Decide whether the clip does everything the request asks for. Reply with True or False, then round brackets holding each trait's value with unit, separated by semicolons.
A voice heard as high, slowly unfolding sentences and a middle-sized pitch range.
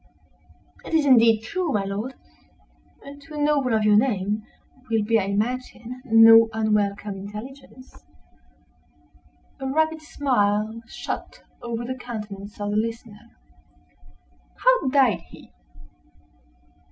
True (230 Hz; 115 wpm; 4.1 semitones)